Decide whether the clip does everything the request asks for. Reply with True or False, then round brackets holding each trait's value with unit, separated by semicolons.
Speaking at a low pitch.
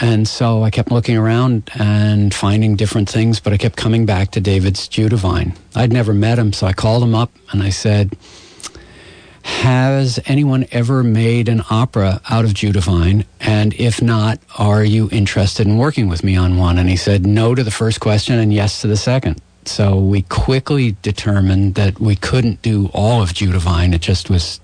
True (105 Hz)